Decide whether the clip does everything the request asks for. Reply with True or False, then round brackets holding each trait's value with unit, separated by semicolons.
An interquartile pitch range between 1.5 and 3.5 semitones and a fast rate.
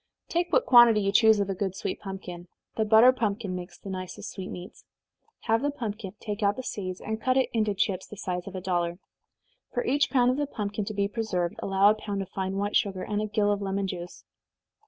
True (2.7 semitones; 235 wpm)